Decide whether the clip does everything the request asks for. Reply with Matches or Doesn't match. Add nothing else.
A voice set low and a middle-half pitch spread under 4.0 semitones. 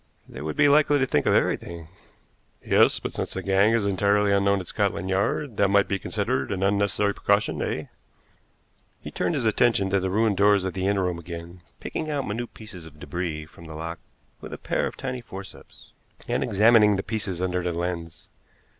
Matches